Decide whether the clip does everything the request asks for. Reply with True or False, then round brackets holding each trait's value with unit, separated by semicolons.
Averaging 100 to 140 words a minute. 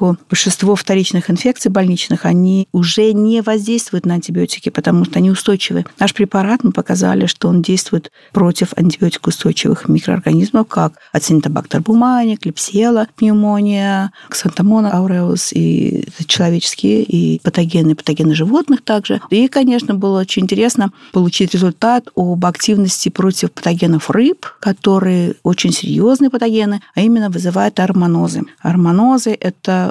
True (120 wpm)